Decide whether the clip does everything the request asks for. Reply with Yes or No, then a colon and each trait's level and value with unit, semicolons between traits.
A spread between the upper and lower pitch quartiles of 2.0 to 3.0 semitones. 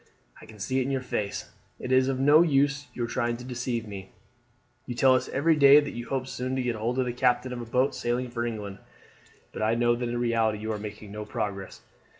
Yes: average, 2.7 semitones